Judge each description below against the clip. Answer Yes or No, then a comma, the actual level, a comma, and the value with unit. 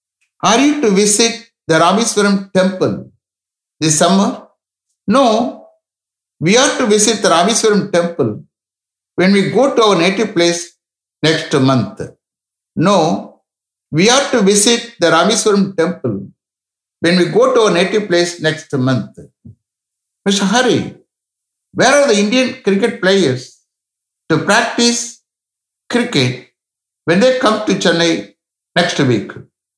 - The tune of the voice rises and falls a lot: Yes, wide, 7.9 semitones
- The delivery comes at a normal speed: No, slow, 125 wpm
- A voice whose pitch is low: No, medium, 180 Hz